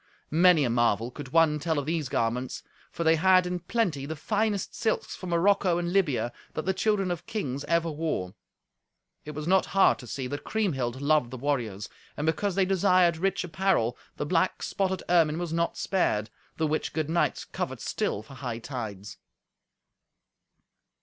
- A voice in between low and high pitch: Yes, medium, 160 Hz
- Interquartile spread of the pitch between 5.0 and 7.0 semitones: Yes, wide, 5.6 semitones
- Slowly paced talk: No, average, 170 wpm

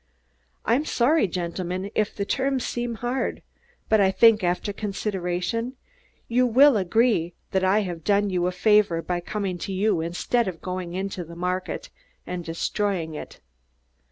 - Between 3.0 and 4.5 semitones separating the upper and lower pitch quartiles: Yes, average, 4.0 semitones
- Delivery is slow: No, average, 155 wpm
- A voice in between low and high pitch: No, high, 195 Hz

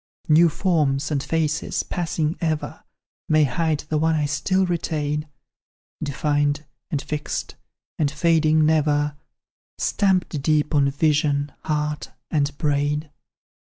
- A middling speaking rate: No, slow, 115 wpm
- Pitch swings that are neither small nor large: No, narrow, 1.5 semitones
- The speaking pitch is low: No, medium, 150 Hz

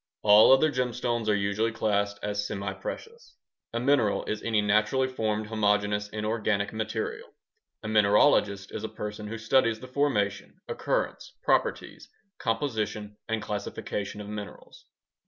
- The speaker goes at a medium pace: No, slow, 130 wpm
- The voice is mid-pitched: No, low, 110 Hz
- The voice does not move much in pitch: Yes, narrow, 2.2 semitones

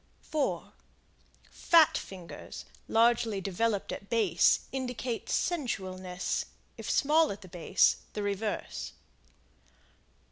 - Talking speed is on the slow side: Yes, slow, 85 wpm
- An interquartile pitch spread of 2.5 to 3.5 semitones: No, average, 4.9 semitones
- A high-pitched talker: Yes, high, 220 Hz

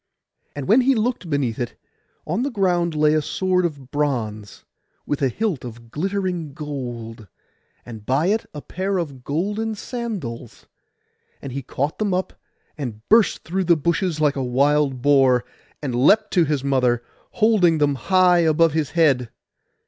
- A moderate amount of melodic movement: No, wide, 6.1 semitones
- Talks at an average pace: Yes, average, 160 wpm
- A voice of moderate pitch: Yes, medium, 150 Hz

